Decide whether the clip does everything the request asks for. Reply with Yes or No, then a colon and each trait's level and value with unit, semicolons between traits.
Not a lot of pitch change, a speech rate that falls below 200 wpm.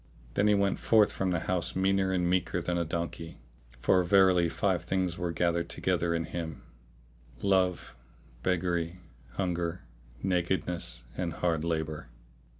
Yes: narrow, 1.9 semitones; average, 145 wpm